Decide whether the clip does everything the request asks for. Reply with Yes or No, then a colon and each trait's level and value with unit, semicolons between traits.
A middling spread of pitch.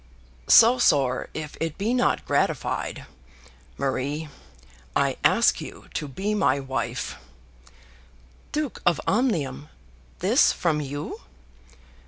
No: wide, 7.5 semitones